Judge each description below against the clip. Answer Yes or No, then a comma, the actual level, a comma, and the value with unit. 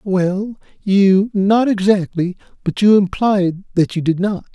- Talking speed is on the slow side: Yes, slow, 130 wpm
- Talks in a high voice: Yes, high, 195 Hz